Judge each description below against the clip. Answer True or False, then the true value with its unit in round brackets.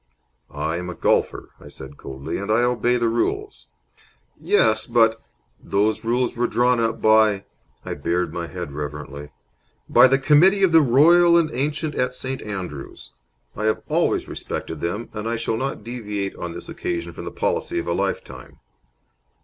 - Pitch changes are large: True (6.4 semitones)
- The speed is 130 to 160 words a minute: False (175 wpm)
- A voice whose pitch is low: True (115 Hz)